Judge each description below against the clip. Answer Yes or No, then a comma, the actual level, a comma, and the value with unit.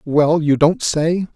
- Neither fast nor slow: Yes, average, 180 wpm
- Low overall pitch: No, medium, 155 Hz